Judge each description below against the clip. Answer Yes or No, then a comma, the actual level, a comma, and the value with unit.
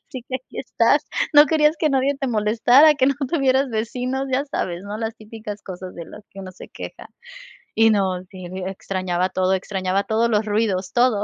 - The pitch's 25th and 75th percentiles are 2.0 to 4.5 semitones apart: No, wide, 5.4 semitones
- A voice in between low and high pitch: No, high, 220 Hz